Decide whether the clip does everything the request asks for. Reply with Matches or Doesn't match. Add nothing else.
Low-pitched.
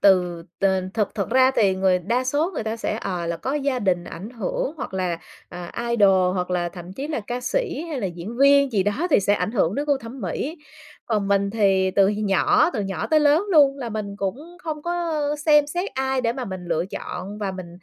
Doesn't match